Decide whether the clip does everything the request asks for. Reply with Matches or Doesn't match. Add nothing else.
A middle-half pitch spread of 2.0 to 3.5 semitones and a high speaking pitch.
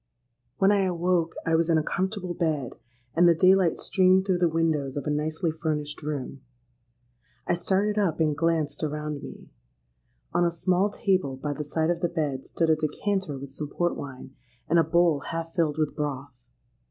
Doesn't match